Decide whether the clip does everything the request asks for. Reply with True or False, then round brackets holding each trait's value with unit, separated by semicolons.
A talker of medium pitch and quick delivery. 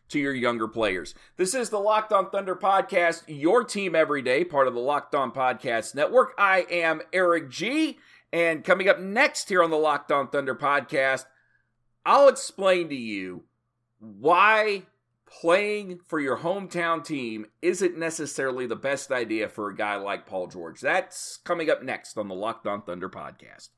False (165 Hz; 170 wpm)